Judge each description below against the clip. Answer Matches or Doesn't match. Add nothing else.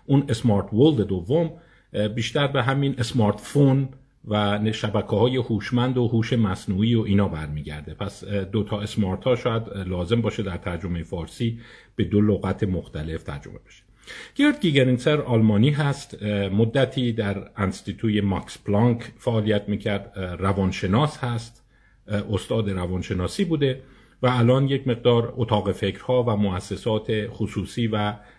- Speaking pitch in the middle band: Doesn't match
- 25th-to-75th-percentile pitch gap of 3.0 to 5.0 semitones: Matches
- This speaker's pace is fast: Doesn't match